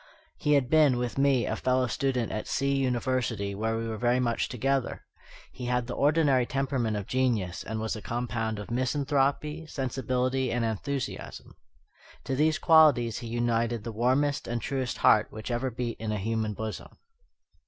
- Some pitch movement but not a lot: Yes, average, 3.2 semitones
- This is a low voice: Yes, low, 125 Hz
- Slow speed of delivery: No, average, 170 wpm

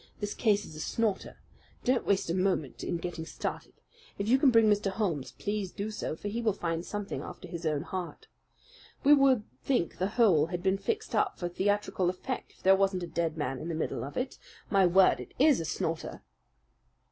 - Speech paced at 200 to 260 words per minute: Yes, fast, 205 wpm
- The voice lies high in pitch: Yes, high, 195 Hz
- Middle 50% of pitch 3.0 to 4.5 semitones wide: Yes, average, 4.1 semitones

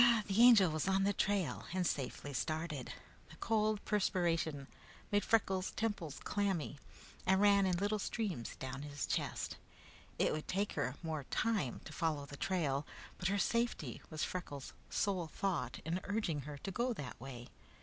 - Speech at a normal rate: Yes, average, 160 wpm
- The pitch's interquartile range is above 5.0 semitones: Yes, wide, 5.6 semitones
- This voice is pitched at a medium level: Yes, medium, 180 Hz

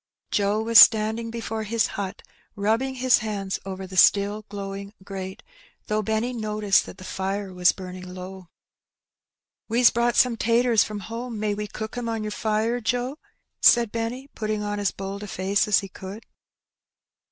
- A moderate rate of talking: Yes, average, 175 wpm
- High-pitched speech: Yes, high, 215 Hz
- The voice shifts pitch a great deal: No, average, 2.7 semitones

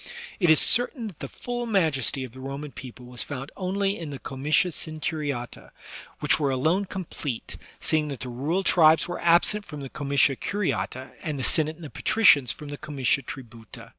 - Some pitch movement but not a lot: Yes, average, 4.7 semitones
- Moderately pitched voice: Yes, medium, 150 Hz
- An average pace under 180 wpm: No, average, 185 wpm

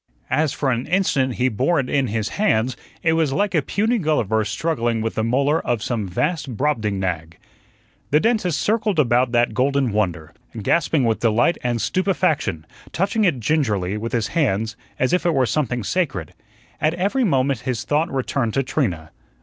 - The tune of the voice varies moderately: No, wide, 6.5 semitones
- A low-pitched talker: Yes, low, 130 Hz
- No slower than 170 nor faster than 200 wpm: Yes, average, 175 wpm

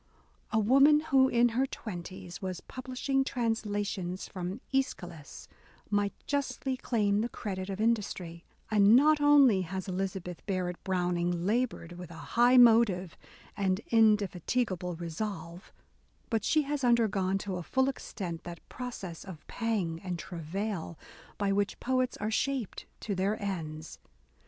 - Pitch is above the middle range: Yes, high, 200 Hz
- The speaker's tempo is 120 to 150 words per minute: Yes, average, 140 wpm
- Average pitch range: Yes, average, 5.0 semitones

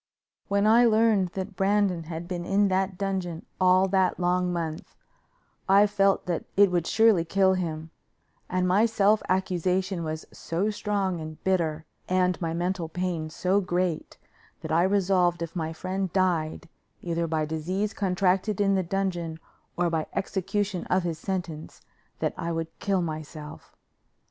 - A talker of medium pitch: Yes, medium, 180 Hz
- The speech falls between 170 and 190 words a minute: No, average, 155 wpm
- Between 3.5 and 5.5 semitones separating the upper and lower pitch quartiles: No, average, 2.7 semitones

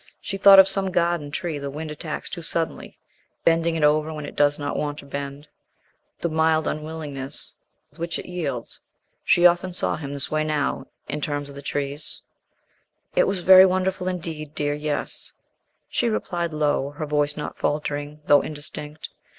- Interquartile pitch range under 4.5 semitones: Yes, average, 2.8 semitones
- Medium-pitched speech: Yes, medium, 155 Hz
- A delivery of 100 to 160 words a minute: No, average, 175 wpm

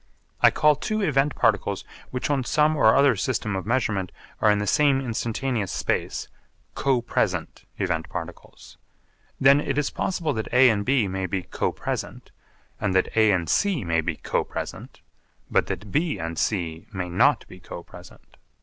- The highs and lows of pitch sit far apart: Yes, wide, 6.5 semitones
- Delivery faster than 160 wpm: Yes, average, 175 wpm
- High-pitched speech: No, low, 115 Hz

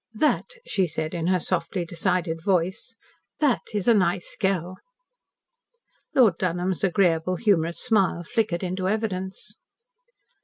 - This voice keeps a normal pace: No, slow, 120 wpm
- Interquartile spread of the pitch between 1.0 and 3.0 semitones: Yes, average, 2.7 semitones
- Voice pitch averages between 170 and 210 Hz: Yes, medium, 185 Hz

